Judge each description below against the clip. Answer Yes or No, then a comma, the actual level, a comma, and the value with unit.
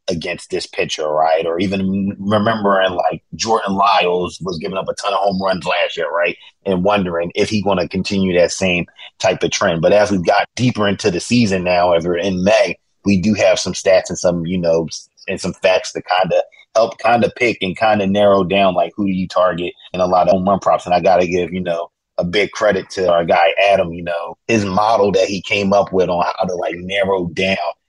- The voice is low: Yes, very low, 95 Hz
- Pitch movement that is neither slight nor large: No, narrow, 2.2 semitones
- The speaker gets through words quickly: Yes, fast, 240 wpm